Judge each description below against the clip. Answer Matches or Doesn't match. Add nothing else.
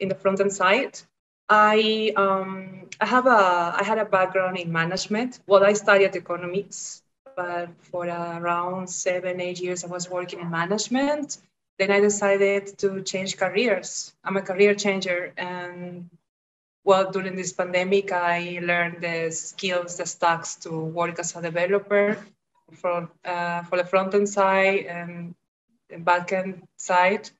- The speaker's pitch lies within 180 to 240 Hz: Matches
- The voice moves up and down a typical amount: Doesn't match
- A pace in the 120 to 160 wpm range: Matches